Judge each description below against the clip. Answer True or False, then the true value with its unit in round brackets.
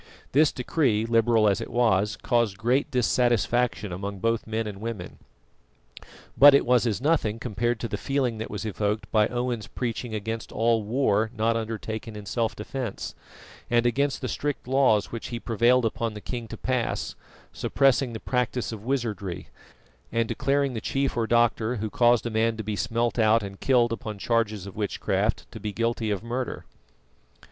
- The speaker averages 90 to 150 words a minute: False (175 wpm)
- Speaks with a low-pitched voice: True (115 Hz)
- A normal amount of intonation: False (2.2 semitones)